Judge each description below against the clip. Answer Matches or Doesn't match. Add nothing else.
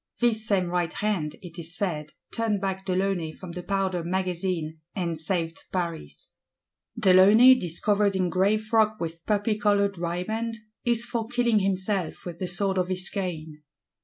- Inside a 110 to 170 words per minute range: Matches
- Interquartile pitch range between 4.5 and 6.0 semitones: Doesn't match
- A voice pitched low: Doesn't match